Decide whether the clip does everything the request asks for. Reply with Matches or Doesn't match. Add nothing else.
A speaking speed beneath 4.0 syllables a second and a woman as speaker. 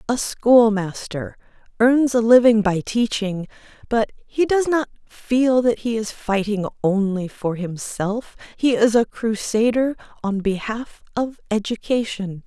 Matches